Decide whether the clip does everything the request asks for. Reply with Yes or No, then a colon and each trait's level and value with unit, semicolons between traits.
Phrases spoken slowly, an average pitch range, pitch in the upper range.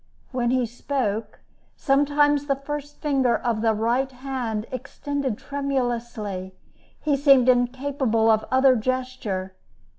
Yes: slow, 115 wpm; average, 3.4 semitones; very high, 255 Hz